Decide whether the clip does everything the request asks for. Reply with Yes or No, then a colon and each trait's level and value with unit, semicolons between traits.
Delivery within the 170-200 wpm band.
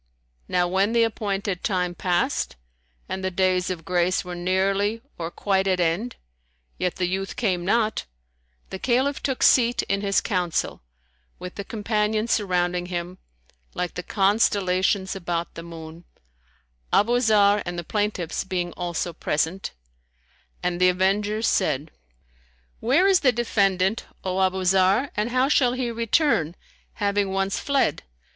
No: average, 140 wpm